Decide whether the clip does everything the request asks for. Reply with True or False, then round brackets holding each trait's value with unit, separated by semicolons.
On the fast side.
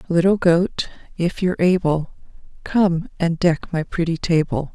False (140 wpm)